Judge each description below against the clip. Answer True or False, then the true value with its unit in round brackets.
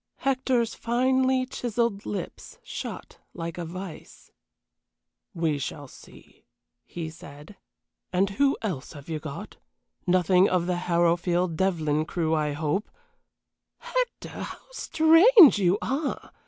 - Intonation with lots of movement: True (6.8 semitones)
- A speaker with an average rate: False (120 wpm)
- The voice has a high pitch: False (180 Hz)